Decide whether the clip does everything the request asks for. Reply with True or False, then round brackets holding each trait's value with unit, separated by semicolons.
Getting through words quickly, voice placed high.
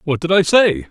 False (265 wpm; 165 Hz)